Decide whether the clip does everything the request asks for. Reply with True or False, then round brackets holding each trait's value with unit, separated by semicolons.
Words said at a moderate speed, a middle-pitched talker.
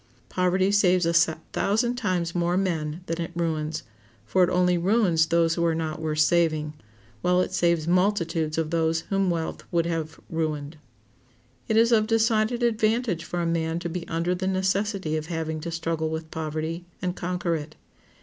True (175 wpm; 170 Hz)